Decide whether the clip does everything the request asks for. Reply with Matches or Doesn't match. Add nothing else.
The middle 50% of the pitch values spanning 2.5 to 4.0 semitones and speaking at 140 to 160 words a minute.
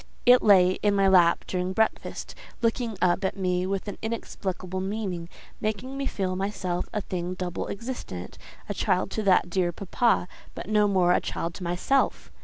Doesn't match